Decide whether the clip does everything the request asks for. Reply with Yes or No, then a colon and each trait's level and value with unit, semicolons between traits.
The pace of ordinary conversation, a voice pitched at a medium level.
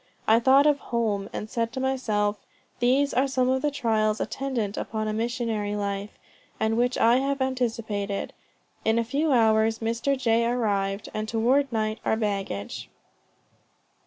No: average, 155 wpm; high, 230 Hz